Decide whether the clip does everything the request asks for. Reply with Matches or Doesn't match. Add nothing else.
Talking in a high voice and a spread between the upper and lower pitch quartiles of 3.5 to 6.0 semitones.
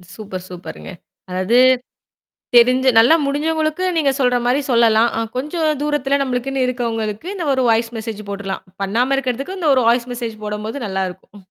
Matches